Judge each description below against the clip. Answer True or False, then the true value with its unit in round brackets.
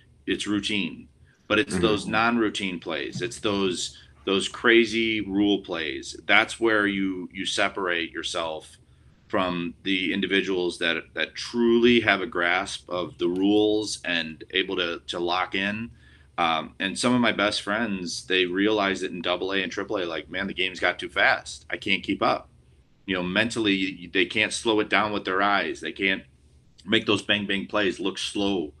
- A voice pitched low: True (100 Hz)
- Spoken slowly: False (175 wpm)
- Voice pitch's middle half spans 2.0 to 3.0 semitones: True (2.6 semitones)